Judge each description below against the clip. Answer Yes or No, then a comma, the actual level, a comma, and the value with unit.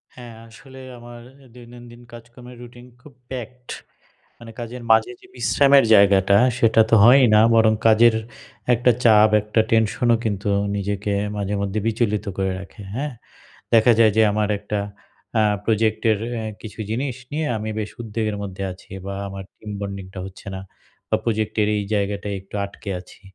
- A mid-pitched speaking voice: No, low, 110 Hz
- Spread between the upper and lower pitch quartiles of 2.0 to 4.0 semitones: Yes, average, 2.8 semitones